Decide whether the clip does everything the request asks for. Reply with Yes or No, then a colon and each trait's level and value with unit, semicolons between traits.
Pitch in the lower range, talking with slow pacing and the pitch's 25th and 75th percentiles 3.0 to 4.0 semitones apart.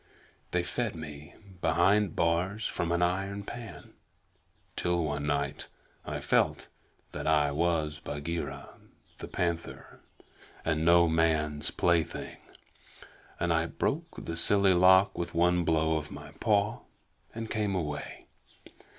Yes: very low, 85 Hz; slow, 125 wpm; average, 3.3 semitones